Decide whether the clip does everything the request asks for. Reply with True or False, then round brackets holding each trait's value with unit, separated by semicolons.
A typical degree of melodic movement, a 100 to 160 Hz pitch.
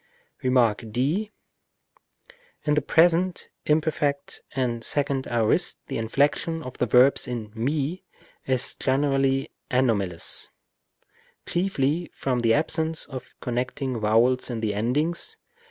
True (4.2 semitones; 135 Hz)